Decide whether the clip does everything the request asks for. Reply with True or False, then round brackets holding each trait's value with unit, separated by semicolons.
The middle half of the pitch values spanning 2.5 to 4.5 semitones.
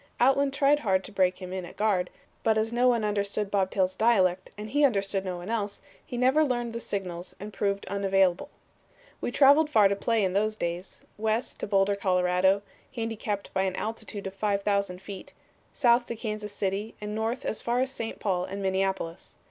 True (3.1 semitones)